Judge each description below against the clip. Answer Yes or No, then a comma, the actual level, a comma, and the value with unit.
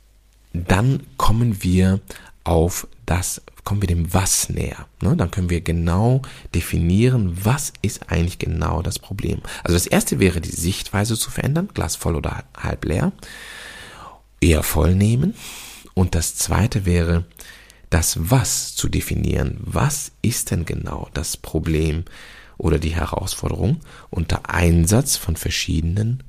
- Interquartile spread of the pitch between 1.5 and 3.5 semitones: No, average, 4.6 semitones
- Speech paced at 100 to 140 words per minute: Yes, average, 130 wpm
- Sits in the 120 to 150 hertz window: No, very low, 95 Hz